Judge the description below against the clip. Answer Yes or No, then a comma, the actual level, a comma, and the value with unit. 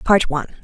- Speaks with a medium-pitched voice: Yes, medium, 170 Hz